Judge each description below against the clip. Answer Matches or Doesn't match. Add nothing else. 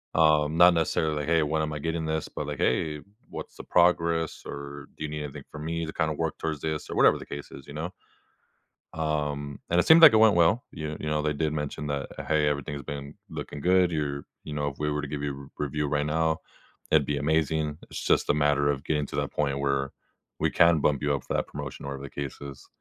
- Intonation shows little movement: Matches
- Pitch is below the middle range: Matches